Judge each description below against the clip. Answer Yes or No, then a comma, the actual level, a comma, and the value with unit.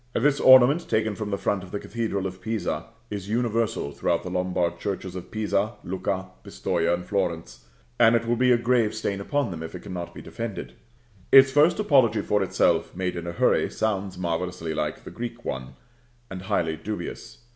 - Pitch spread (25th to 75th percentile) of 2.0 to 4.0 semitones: No, average, 4.4 semitones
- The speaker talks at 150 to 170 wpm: No, average, 190 wpm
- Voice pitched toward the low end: Yes, low, 100 Hz